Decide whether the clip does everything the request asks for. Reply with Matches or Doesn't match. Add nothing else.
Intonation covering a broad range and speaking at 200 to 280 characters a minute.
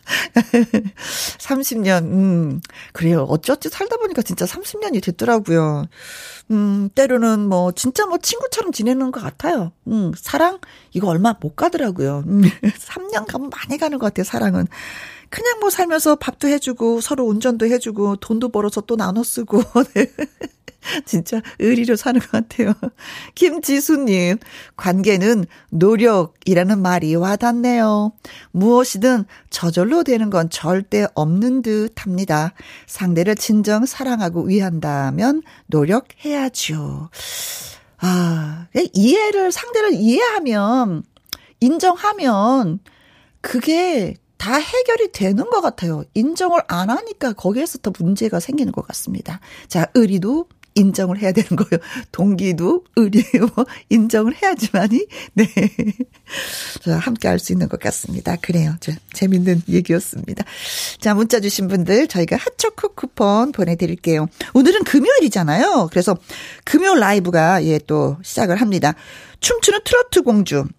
Matches